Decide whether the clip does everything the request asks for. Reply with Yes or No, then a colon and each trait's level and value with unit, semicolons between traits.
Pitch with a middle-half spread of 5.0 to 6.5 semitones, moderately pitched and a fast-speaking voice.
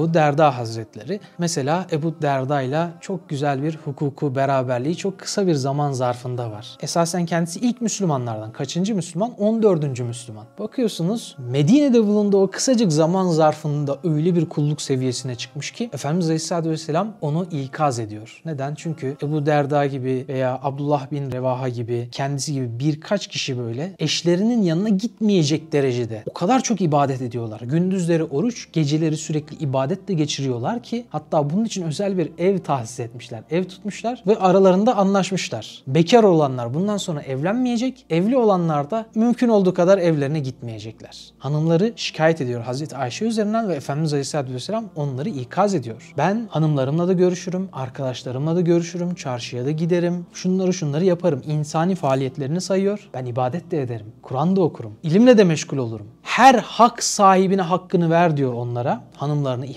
Yes: wide, 5.5 semitones; medium, 160 Hz; fast, 150 wpm